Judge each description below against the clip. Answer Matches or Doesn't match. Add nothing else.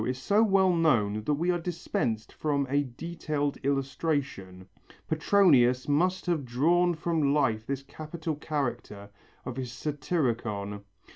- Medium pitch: Matches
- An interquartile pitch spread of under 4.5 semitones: Doesn't match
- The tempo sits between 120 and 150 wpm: Matches